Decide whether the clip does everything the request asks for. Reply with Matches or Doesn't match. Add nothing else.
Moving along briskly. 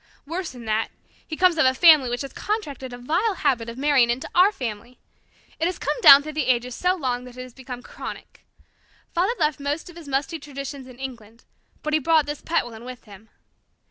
Matches